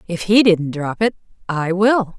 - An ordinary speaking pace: Yes, average, 190 wpm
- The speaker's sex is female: Yes, female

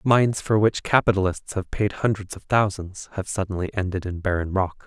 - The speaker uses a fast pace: No, average, 185 wpm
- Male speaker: Yes, male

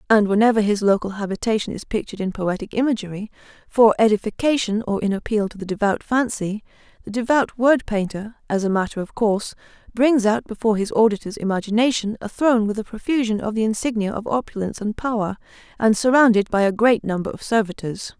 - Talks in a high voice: Yes, high, 215 Hz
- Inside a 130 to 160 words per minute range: No, average, 180 wpm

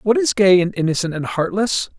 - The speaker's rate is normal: No, fast, 210 wpm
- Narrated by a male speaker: Yes, male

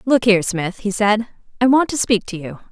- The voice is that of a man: No, female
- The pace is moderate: No, fast, 245 wpm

